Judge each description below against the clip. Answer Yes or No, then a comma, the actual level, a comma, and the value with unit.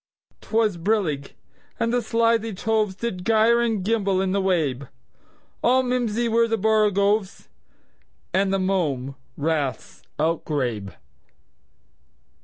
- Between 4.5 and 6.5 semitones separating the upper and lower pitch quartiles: Yes, wide, 5.5 semitones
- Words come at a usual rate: No, slow, 100 wpm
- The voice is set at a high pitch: Yes, high, 200 Hz